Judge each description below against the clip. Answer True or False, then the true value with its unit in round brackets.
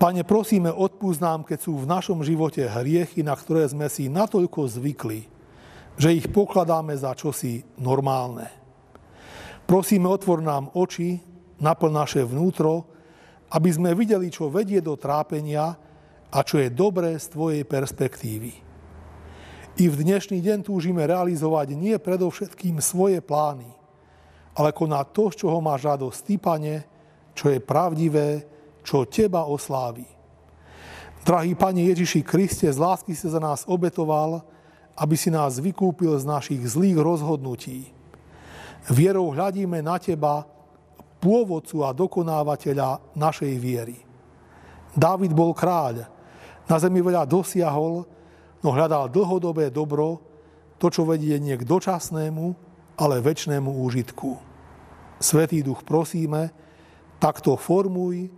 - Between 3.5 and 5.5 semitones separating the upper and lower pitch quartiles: True (4.0 semitones)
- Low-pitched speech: False (160 Hz)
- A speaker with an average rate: True (120 wpm)